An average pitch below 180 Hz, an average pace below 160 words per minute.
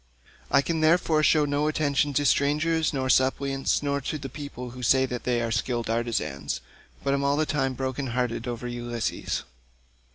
No: low, 135 Hz; average, 170 wpm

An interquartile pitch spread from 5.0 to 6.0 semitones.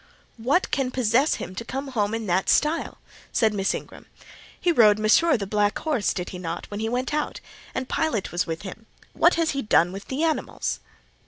Yes: wide, 5.5 semitones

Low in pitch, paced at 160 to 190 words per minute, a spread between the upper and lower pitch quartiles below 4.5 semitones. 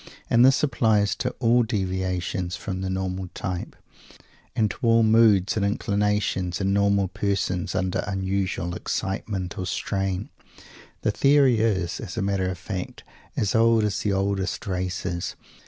No: low, 100 Hz; average, 145 wpm; narrow, 2.6 semitones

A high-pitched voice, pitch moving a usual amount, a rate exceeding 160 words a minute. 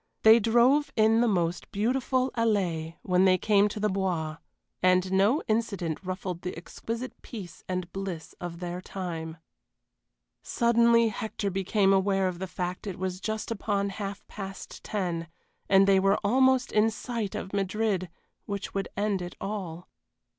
No: high, 195 Hz; average, 3.2 semitones; average, 155 wpm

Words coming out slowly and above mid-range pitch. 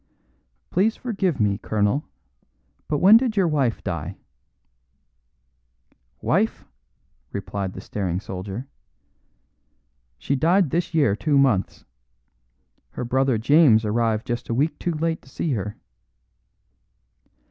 No: slow, 115 wpm; low, 135 Hz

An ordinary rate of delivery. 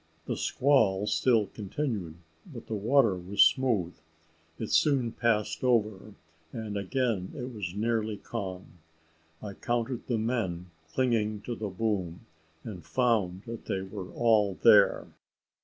No: slow, 130 wpm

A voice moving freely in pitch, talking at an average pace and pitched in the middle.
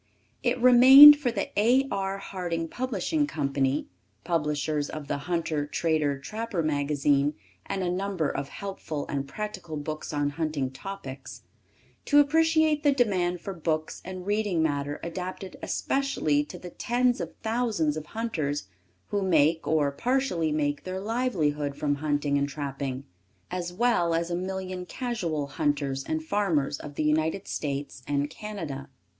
Yes: wide, 6.0 semitones; average, 145 wpm; medium, 165 Hz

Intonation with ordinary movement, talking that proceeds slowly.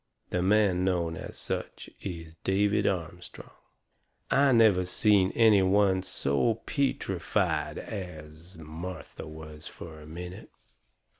Yes: average, 3.7 semitones; slow, 115 wpm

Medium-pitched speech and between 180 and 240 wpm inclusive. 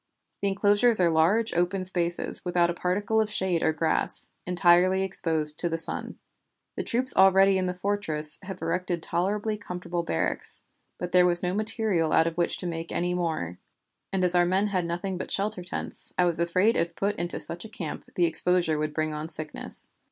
Yes: medium, 180 Hz; average, 195 wpm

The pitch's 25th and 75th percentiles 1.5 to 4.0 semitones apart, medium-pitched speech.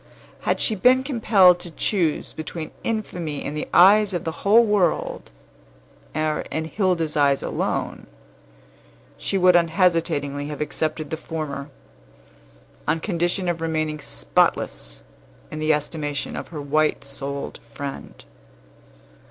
Yes: average, 3.3 semitones; medium, 160 Hz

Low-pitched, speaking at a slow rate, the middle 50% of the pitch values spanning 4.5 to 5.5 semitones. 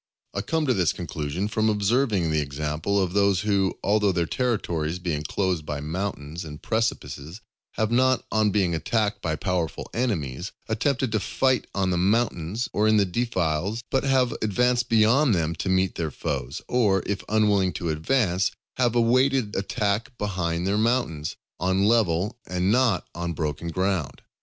No: low, 100 Hz; average, 160 wpm; average, 5.0 semitones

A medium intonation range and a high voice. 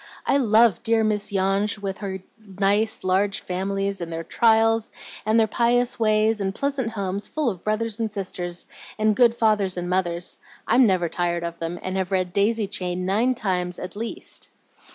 Yes: average, 3.2 semitones; high, 200 Hz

